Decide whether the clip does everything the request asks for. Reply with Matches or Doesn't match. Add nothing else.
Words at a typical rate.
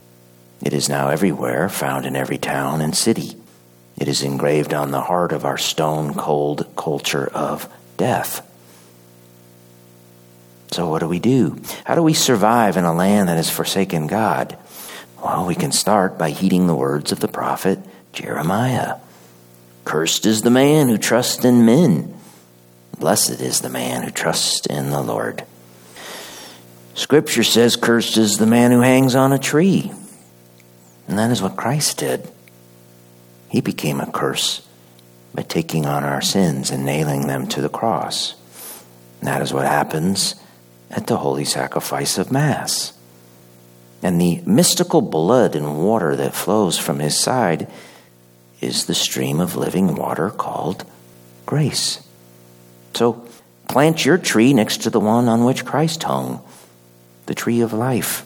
Matches